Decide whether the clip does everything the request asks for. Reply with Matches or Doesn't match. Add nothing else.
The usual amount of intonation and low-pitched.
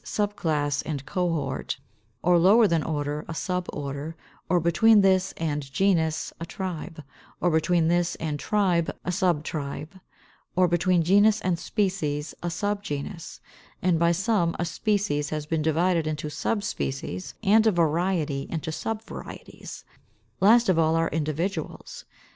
Doesn't match